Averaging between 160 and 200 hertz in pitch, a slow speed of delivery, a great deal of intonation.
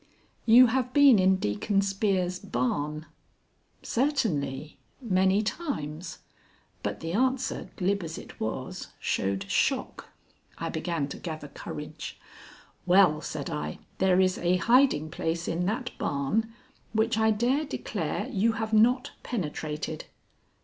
Yes: high, 190 Hz; slow, 125 wpm; wide, 6.4 semitones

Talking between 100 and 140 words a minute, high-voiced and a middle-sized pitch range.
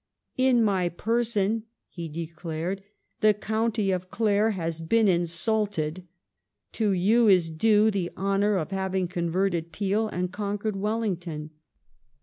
Yes: slow, 135 wpm; high, 195 Hz; average, 3.8 semitones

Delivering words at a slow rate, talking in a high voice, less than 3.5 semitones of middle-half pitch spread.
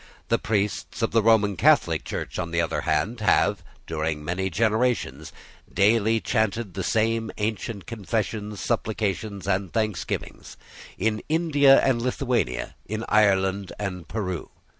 No: slow, 130 wpm; low, 105 Hz; average, 3.0 semitones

